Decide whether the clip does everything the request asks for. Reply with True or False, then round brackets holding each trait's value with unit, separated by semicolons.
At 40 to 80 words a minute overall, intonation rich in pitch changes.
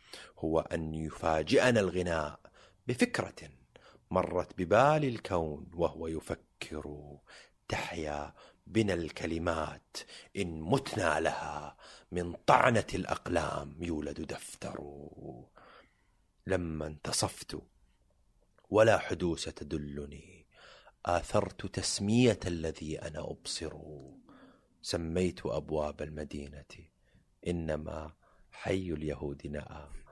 False (75 wpm; 3.1 semitones)